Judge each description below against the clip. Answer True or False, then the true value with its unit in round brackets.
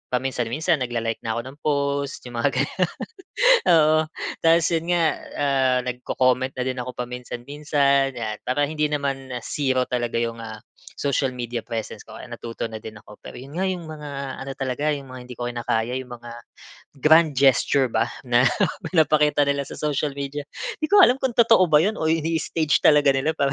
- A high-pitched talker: False (135 Hz)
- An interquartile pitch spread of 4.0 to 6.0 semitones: False (3.6 semitones)